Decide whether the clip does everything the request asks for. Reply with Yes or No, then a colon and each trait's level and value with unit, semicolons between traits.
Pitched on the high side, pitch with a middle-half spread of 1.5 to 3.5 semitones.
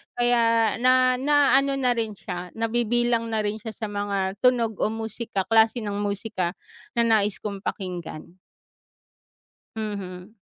Yes: high, 220 Hz; average, 3.0 semitones